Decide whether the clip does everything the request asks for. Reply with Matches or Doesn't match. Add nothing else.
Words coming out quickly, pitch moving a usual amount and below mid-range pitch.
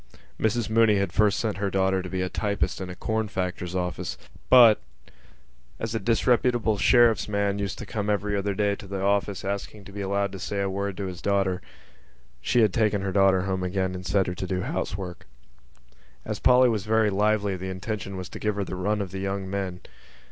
Doesn't match